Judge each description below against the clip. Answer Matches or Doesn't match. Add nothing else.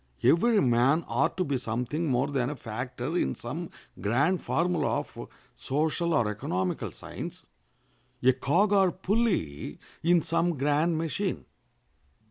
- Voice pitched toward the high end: Doesn't match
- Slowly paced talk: Matches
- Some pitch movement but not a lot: Doesn't match